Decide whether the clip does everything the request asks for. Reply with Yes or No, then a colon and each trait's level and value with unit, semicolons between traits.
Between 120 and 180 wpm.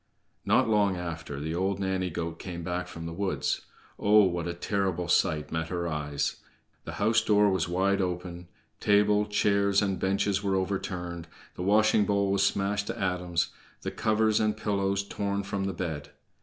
Yes: average, 170 wpm